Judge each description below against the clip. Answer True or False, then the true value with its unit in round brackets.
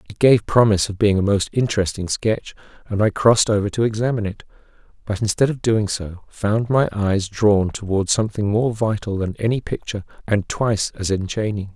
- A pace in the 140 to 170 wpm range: False (185 wpm)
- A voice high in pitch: False (105 Hz)